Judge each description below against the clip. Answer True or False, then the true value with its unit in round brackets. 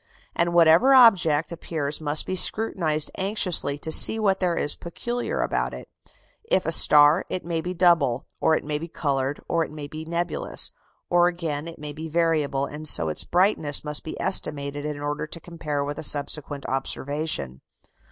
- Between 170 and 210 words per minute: True (180 wpm)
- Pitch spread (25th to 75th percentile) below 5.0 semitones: True (2.9 semitones)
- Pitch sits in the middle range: True (155 Hz)